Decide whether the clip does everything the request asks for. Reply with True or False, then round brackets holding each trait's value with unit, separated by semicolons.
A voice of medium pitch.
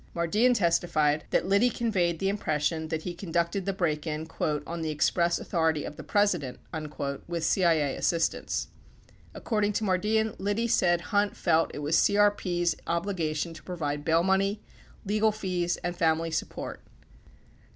True (175 Hz)